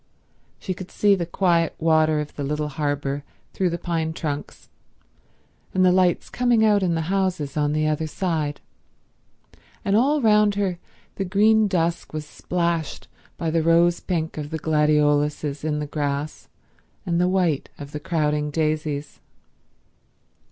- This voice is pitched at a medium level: Yes, medium, 160 Hz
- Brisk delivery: No, average, 150 wpm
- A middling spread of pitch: Yes, average, 3.5 semitones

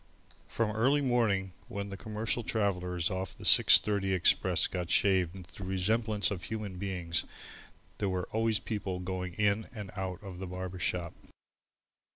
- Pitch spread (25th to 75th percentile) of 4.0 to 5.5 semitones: No, average, 2.7 semitones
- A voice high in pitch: No, very low, 95 Hz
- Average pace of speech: Yes, average, 155 wpm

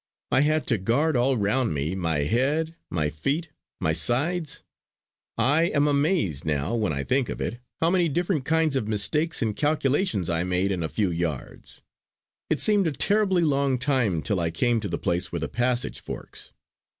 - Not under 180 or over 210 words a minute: Yes, average, 185 wpm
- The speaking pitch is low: Yes, low, 125 Hz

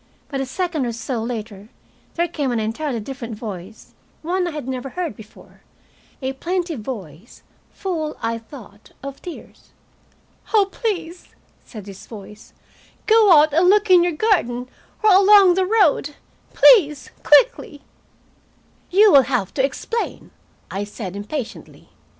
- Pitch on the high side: Yes, very high, 280 Hz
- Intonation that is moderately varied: No, wide, 7.8 semitones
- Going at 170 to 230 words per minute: No, average, 140 wpm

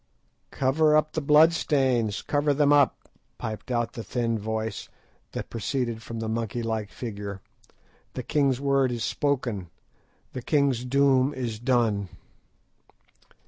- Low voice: Yes, low, 125 Hz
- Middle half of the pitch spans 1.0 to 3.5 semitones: No, average, 3.9 semitones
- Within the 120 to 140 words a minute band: Yes, slow, 135 wpm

